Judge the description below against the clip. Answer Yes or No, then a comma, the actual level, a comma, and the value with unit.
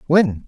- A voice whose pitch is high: No, medium, 145 Hz